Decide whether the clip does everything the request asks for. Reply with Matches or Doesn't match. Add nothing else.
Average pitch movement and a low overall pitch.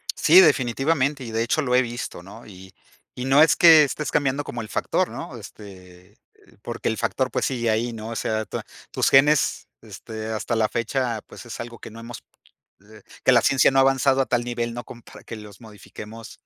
Matches